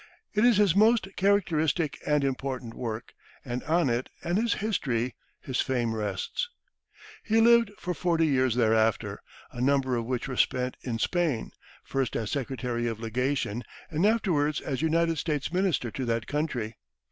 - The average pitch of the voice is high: No, low, 135 Hz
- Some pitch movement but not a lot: No, wide, 6.2 semitones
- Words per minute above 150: Yes, average, 160 wpm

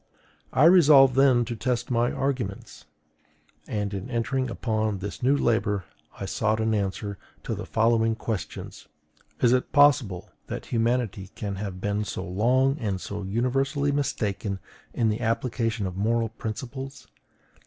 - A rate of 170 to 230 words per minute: No, average, 145 wpm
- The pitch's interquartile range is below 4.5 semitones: Yes, average, 3.8 semitones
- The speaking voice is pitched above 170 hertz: No, low, 115 Hz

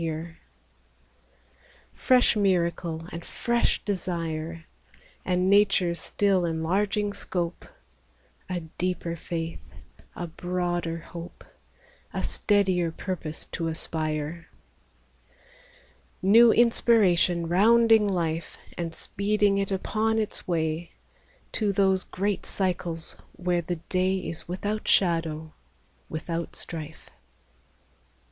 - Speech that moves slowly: Yes, slow, 100 wpm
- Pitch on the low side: No, medium, 175 Hz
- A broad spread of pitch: No, average, 3.2 semitones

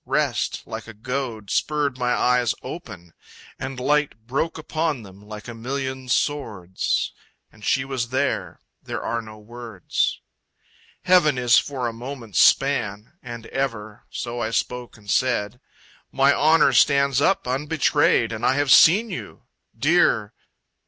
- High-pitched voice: No, low, 125 Hz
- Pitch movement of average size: Yes, average, 3.8 semitones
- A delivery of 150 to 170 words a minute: No, average, 140 wpm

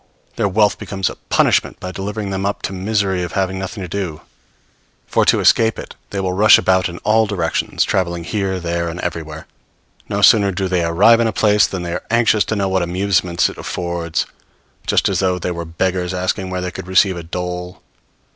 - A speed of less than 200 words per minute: No, fast, 205 wpm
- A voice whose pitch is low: Yes, very low, 95 Hz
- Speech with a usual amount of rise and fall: No, narrow, 2.3 semitones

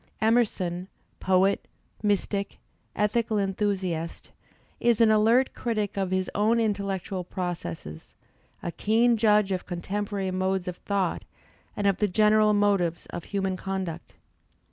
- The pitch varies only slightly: Yes, narrow, 2.3 semitones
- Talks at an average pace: No, slow, 125 wpm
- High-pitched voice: Yes, high, 200 Hz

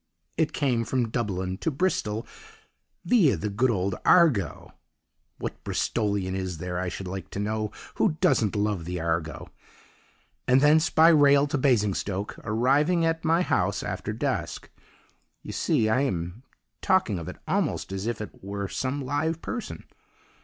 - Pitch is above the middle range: No, low, 110 Hz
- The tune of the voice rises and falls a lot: Yes, wide, 7.0 semitones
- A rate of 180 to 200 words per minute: No, average, 155 wpm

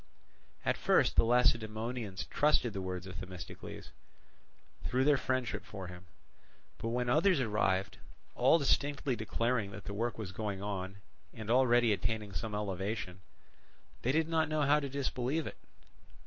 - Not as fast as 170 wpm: Yes, average, 150 wpm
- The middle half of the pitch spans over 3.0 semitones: Yes, average, 4.7 semitones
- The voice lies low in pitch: Yes, low, 115 Hz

